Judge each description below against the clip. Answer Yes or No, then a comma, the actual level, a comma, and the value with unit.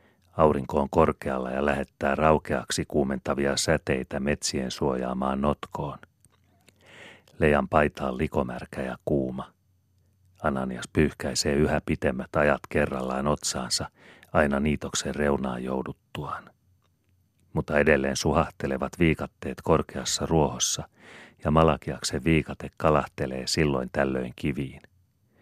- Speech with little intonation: No, average, 3.2 semitones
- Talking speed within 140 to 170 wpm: No, slow, 95 wpm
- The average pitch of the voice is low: Yes, very low, 75 Hz